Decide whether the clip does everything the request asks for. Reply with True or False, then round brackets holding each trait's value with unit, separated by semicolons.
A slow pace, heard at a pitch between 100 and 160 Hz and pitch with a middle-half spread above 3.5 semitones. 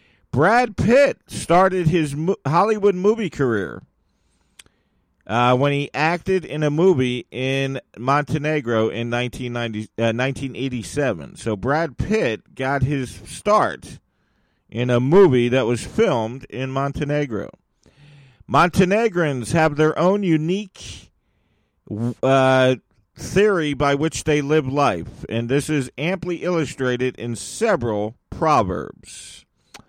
True (105 wpm; 140 Hz; 5.2 semitones)